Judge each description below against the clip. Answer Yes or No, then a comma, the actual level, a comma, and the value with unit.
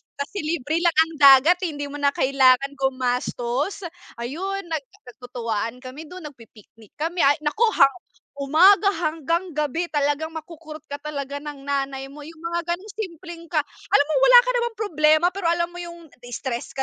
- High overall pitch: Yes, very high, 305 Hz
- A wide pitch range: No, average, 3.8 semitones